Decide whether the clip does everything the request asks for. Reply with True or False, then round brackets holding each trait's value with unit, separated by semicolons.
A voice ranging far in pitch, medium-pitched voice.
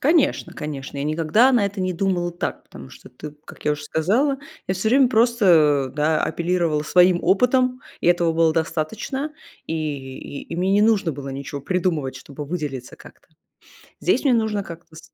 True (5.7 semitones; 175 Hz)